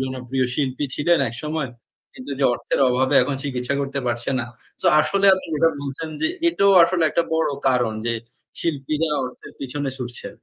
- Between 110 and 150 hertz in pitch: Yes, medium, 140 Hz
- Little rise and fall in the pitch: No, average, 3.8 semitones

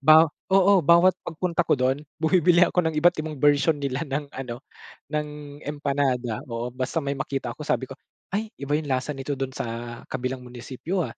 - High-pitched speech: No, medium, 145 Hz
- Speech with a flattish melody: No, average, 3.8 semitones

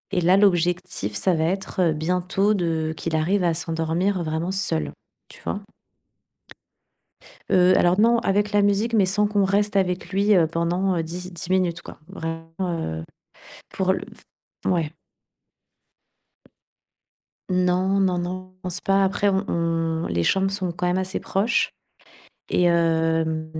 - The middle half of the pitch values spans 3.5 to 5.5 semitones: No, average, 2.8 semitones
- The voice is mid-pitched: Yes, medium, 180 Hz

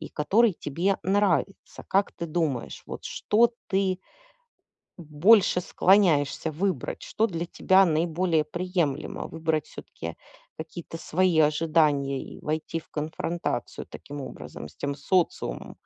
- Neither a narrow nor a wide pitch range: Yes, average, 3.6 semitones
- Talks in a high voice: No, medium, 165 Hz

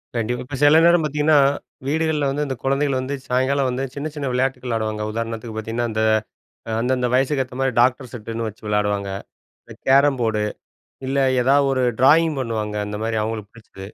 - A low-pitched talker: Yes, low, 125 Hz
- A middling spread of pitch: Yes, average, 3.8 semitones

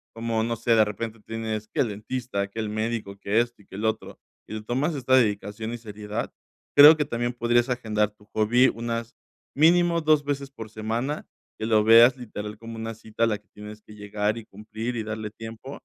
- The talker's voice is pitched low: Yes, low, 115 Hz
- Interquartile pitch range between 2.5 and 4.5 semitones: No, narrow, 2.1 semitones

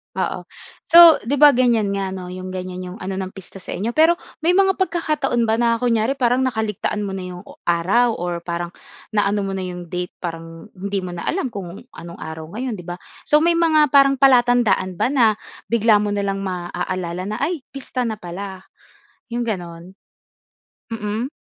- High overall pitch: Yes, high, 205 Hz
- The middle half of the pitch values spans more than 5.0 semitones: Yes, wide, 5.4 semitones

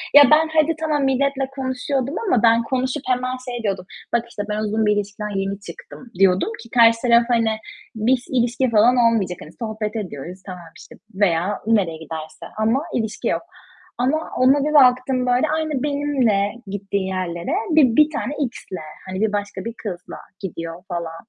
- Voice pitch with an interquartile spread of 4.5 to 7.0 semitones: Yes, average, 4.8 semitones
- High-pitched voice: Yes, high, 230 Hz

